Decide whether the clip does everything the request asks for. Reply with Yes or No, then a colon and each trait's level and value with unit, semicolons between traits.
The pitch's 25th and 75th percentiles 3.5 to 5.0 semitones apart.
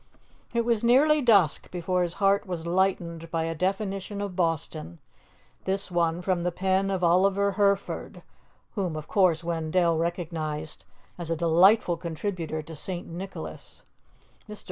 No: average, 3.0 semitones